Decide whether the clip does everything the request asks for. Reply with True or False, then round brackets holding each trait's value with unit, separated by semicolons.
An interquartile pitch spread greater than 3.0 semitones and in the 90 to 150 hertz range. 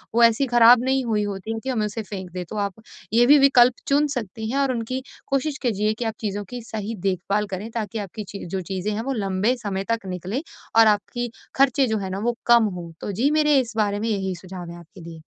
False (3.7 semitones; 220 Hz)